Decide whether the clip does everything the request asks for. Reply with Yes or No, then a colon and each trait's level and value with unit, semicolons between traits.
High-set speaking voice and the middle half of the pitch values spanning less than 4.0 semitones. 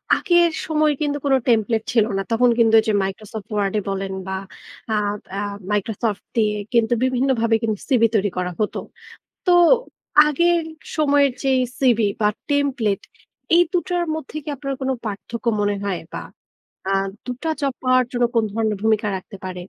No: high, 230 Hz; average, 4.7 semitones